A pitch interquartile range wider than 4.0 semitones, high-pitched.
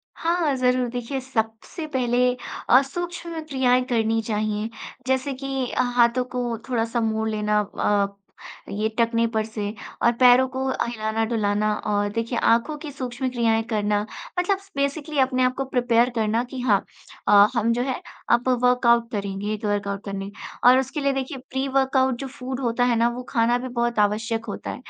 No: average, 3.1 semitones; high, 240 Hz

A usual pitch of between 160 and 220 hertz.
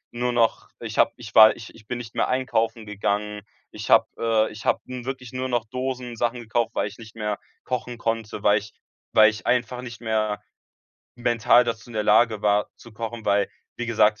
No: low, 115 Hz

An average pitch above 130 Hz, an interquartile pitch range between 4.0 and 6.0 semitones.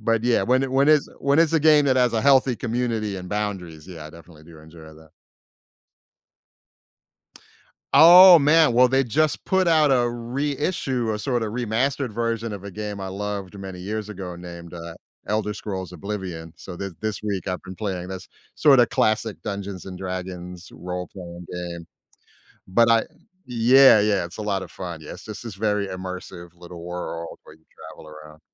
No: low, 105 Hz; average, 5.3 semitones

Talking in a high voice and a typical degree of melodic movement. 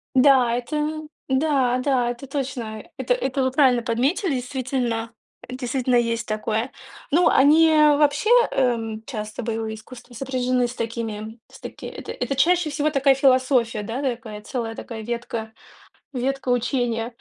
Yes: very high, 250 Hz; average, 3.0 semitones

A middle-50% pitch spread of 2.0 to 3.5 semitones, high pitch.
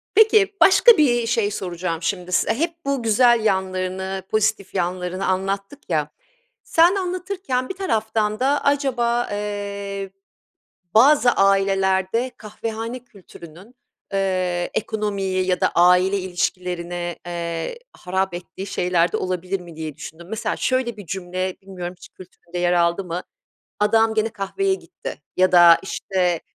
No: average, 4.2 semitones; high, 195 Hz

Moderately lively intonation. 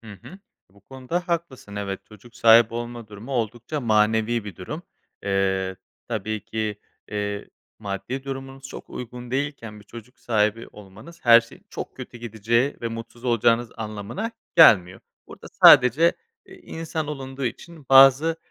Yes: average, 4.1 semitones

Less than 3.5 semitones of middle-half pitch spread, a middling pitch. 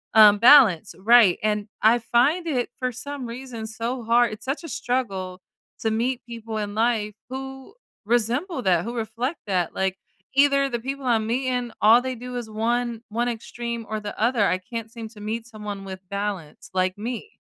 No: average, 2.8 semitones; high, 230 Hz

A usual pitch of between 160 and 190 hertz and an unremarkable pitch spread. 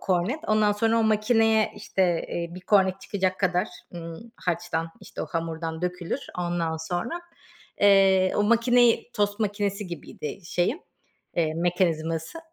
Yes: medium, 185 Hz; average, 3.9 semitones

